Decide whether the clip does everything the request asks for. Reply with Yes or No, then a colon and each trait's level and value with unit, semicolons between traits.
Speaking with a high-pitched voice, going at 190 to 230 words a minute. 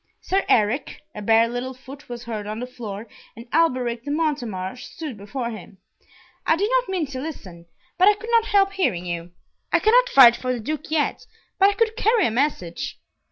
Yes: very high, 255 Hz; average, 200 wpm